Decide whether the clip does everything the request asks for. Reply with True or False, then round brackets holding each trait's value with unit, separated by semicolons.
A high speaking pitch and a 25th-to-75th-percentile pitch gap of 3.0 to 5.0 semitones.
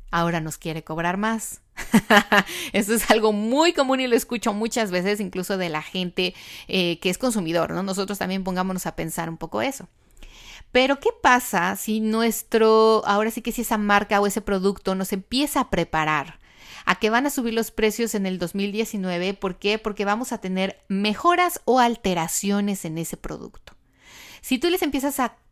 True (205 Hz; 3.9 semitones)